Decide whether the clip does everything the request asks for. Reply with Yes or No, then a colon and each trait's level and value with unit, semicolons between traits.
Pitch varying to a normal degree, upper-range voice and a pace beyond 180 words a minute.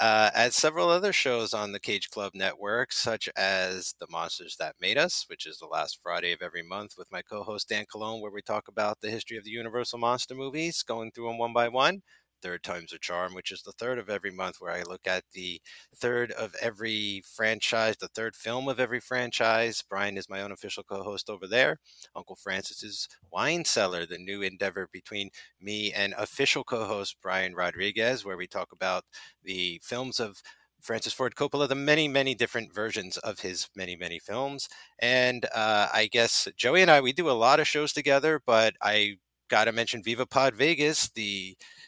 No: average, 4.2 semitones; low, 110 Hz; average, 200 wpm